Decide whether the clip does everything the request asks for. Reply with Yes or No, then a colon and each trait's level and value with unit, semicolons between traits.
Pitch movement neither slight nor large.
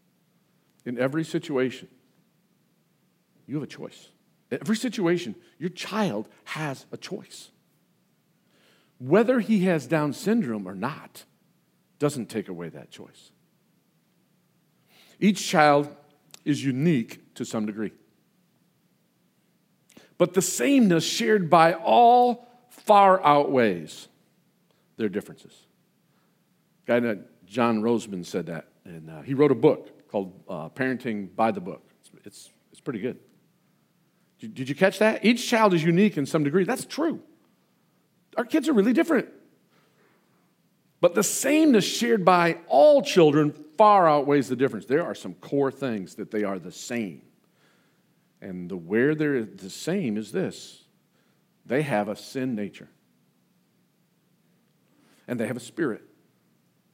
No: wide, 6.6 semitones